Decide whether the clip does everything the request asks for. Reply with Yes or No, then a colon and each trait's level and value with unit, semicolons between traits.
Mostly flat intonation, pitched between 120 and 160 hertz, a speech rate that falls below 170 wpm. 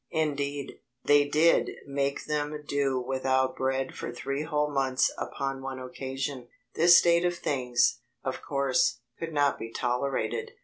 Yes: narrow, 1.9 semitones; medium, 140 Hz; average, 140 wpm